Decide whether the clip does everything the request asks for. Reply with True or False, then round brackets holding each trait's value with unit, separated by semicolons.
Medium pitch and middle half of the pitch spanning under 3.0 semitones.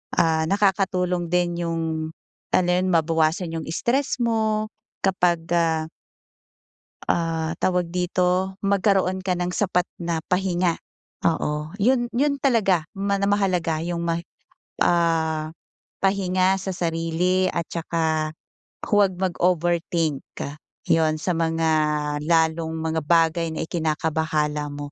True (175 Hz; 2.5 semitones)